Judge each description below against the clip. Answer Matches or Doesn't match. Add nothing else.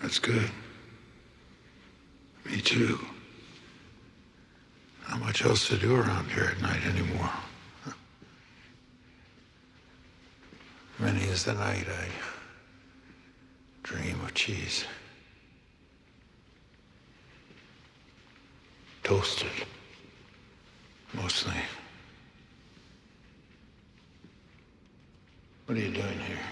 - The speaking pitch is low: Matches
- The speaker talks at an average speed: Doesn't match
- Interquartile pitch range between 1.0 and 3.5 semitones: Doesn't match